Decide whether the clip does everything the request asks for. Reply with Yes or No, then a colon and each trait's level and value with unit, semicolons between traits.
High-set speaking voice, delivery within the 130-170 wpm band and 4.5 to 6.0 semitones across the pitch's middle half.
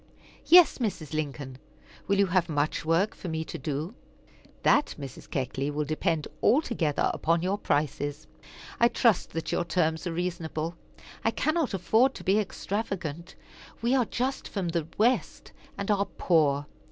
No: medium, 170 Hz; average, 155 wpm; average, 5.1 semitones